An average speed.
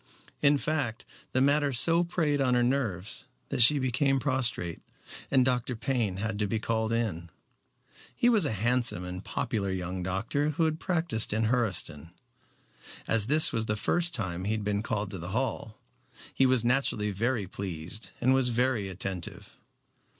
Yes: average, 165 wpm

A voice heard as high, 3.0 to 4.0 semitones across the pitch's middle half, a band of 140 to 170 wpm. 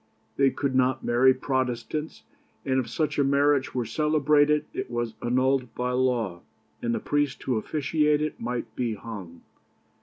No: low, 130 Hz; average, 3.5 semitones; average, 150 wpm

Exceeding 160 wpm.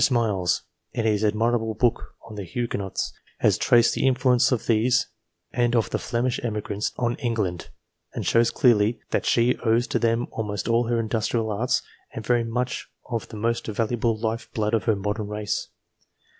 Yes: average, 170 wpm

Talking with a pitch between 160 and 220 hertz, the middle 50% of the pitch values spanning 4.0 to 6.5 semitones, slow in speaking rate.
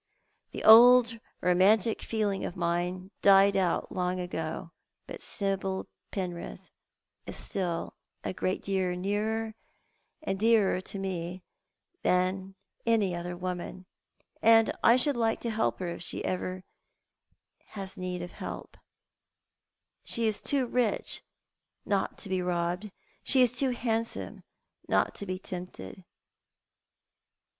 No: high, 190 Hz; average, 3.5 semitones; slow, 130 wpm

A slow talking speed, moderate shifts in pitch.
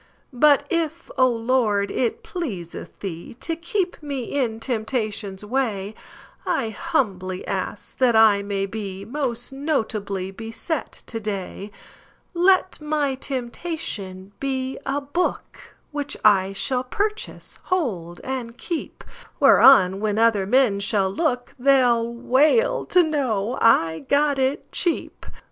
No: slow, 110 wpm; wide, 6.0 semitones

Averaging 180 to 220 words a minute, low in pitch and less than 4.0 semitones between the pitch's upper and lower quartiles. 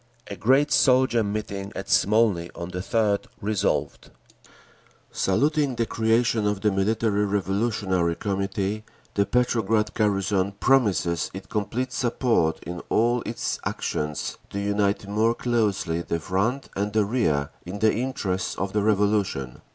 No: slow, 135 wpm; low, 105 Hz; average, 2.9 semitones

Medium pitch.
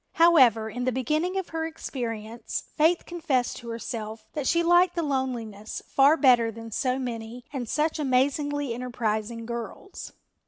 No: very high, 255 Hz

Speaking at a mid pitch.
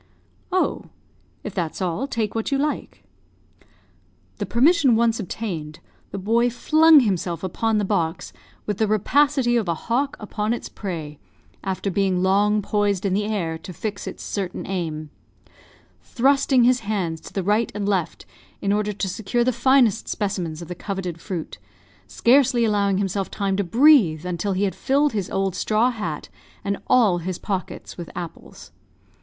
No: high, 205 Hz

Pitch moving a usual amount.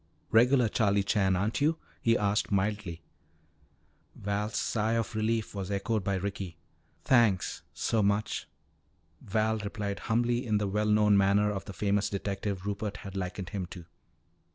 No: narrow, 1.8 semitones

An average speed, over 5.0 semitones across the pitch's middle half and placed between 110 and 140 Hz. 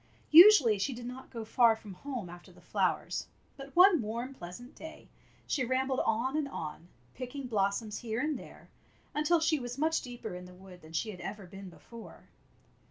No: average, 185 wpm; wide, 5.6 semitones; high, 240 Hz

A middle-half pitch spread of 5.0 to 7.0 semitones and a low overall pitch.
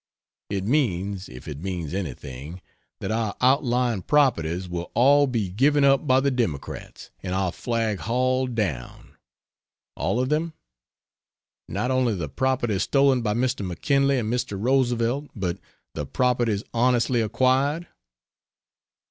Yes: wide, 5.4 semitones; low, 120 Hz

